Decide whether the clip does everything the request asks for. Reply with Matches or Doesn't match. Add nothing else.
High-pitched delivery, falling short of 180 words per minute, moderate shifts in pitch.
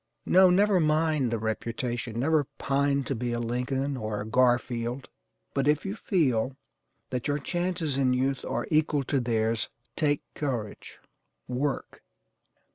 Doesn't match